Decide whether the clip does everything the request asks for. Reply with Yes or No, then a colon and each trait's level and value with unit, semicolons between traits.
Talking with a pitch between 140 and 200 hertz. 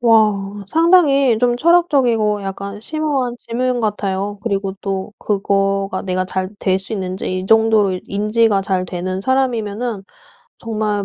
No: high, 210 Hz